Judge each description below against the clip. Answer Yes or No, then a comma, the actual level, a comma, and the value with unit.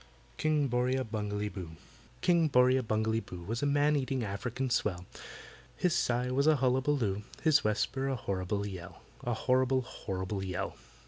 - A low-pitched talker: Yes, low, 125 Hz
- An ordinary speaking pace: Yes, average, 150 wpm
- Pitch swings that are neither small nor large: Yes, average, 4.6 semitones